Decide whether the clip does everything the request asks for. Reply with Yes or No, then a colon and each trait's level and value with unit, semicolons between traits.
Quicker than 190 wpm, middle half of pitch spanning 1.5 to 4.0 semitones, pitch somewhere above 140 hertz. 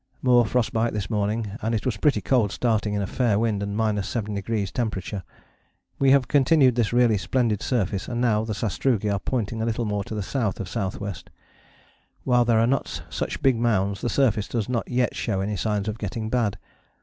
No: average, 200 wpm; average, 2.9 semitones; low, 110 Hz